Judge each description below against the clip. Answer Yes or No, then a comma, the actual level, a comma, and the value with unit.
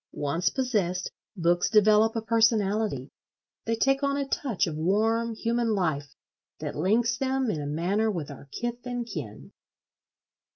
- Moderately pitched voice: No, high, 215 Hz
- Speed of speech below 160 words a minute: Yes, average, 150 wpm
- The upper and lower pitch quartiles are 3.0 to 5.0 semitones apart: No, wide, 5.4 semitones